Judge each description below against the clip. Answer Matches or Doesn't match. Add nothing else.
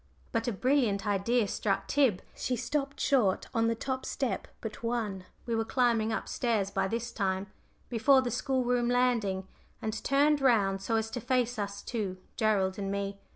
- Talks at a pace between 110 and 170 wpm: Doesn't match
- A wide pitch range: Doesn't match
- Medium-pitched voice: Doesn't match